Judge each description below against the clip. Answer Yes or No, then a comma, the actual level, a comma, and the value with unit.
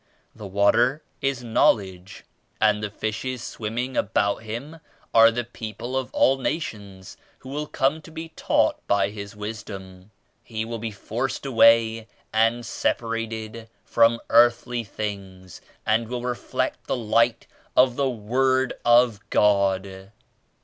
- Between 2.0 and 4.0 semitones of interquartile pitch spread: Yes, average, 2.9 semitones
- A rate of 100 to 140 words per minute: Yes, slow, 135 wpm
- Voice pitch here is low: Yes, low, 115 Hz